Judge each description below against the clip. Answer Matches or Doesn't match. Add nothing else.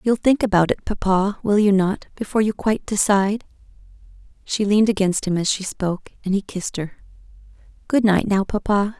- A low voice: Doesn't match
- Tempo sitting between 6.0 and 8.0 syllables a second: Doesn't match